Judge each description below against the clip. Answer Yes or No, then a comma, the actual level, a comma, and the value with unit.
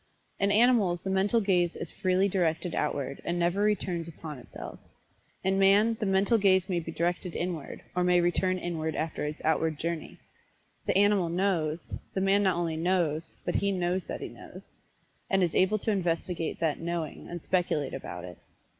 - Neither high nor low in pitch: Yes, medium, 175 Hz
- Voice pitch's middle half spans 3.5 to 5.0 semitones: No, average, 2.8 semitones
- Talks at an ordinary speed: Yes, average, 180 wpm